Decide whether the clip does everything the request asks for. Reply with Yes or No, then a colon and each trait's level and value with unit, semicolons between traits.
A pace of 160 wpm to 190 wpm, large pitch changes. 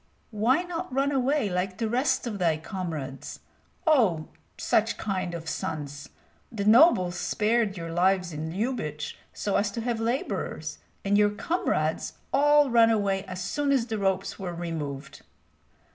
No: average, 150 wpm; wide, 5.7 semitones